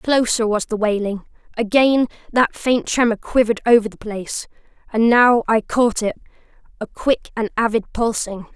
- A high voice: Yes, high, 225 Hz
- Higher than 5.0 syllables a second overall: No, 4.8 syllables/s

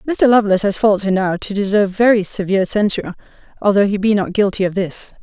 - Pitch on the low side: No, high, 200 Hz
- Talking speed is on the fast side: No, average, 195 wpm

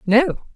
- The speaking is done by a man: No, female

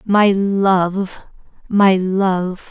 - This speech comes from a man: No, female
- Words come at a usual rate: No, slow, 90 wpm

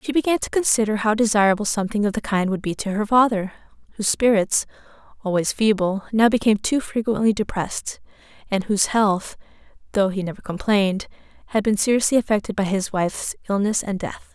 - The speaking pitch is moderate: No, high, 210 Hz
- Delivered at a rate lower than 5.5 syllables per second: No, 6.0 syllables/s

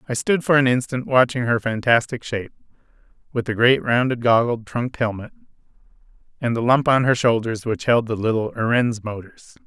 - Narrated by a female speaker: No, male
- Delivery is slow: No, average, 175 wpm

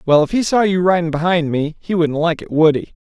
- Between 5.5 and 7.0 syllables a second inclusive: Yes, 5.7 syllables/s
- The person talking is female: No, male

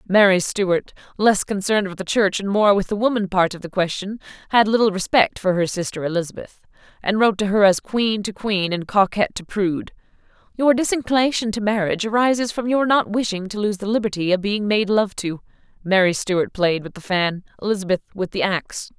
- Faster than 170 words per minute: Yes, average, 200 wpm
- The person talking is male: No, female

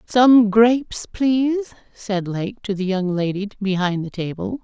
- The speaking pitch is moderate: No, high, 210 Hz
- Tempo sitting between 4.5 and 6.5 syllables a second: No, 4.1 syllables/s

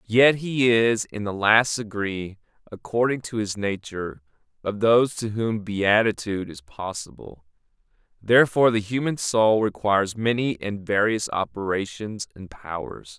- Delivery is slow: Yes, slow, 130 wpm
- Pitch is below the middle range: Yes, low, 105 Hz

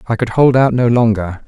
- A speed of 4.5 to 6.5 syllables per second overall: Yes, 5.3 syllables/s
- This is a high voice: No, low, 120 Hz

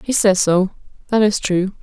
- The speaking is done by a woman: Yes, female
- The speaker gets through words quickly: No, average, 195 wpm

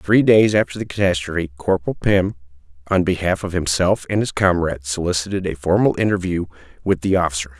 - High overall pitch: No, very low, 90 Hz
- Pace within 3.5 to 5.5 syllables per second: No, 6.1 syllables/s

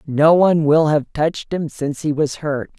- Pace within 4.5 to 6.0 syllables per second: Yes, 5.2 syllables/s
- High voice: No, medium, 150 Hz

